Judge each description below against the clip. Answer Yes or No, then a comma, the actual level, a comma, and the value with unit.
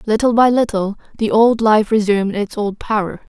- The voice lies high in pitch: Yes, high, 215 Hz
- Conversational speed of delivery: Yes, average, 180 wpm